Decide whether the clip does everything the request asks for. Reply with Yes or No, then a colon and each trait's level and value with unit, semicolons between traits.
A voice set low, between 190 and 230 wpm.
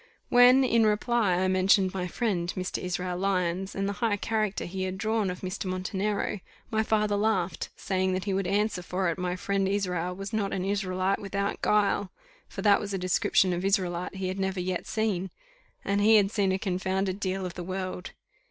No: high, 195 Hz; average, 200 wpm